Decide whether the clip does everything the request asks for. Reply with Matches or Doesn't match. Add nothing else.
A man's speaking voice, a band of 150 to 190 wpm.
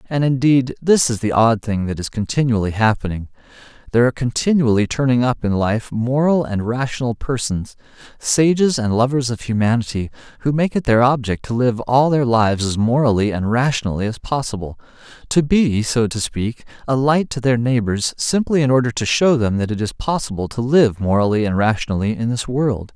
Matches